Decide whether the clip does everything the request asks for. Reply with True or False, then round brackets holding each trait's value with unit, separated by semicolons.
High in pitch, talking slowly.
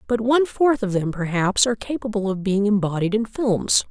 False (215 Hz; 200 wpm)